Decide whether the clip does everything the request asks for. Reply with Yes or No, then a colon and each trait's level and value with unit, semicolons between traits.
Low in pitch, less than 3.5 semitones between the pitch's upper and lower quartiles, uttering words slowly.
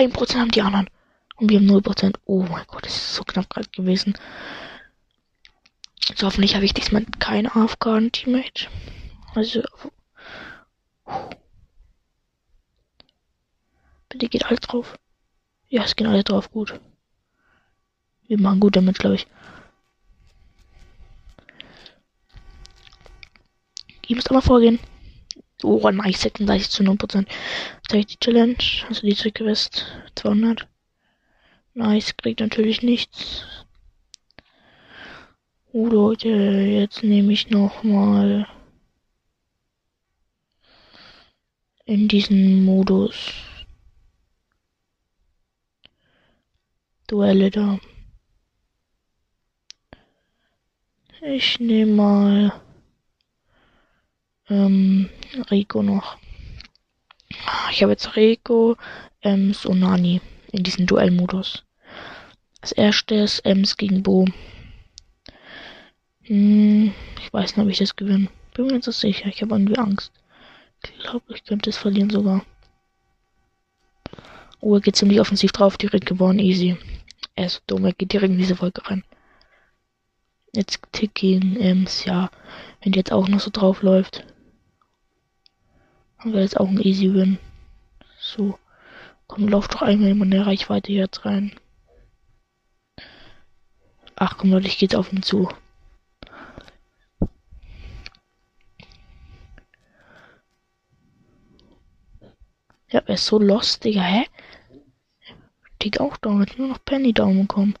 No: high, 200 Hz; narrow, 2.4 semitones; slow, 110 wpm